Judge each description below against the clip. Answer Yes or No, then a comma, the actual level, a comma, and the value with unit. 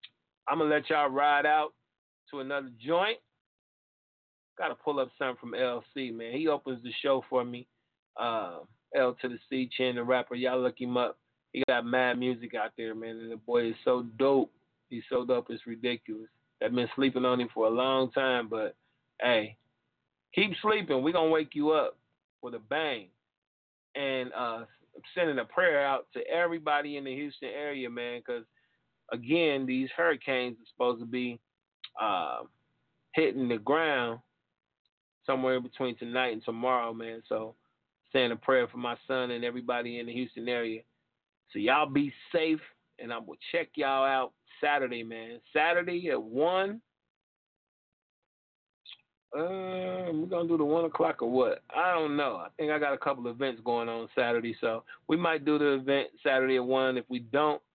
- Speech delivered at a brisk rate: No, average, 180 wpm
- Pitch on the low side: Yes, low, 130 Hz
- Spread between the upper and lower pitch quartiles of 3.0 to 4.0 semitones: Yes, average, 3.5 semitones